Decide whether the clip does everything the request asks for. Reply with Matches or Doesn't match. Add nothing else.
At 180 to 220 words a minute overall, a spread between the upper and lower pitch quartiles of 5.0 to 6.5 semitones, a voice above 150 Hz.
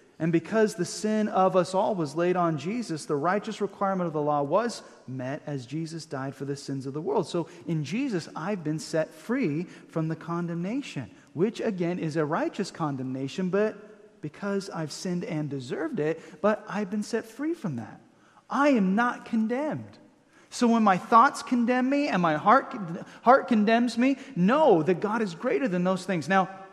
Matches